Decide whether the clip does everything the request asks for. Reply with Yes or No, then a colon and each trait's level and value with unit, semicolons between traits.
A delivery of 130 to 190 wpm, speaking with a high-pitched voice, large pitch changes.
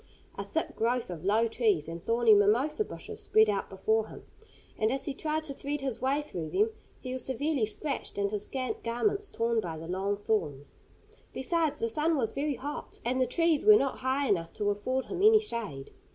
No: fast, 205 wpm; high, 240 Hz; wide, 5.9 semitones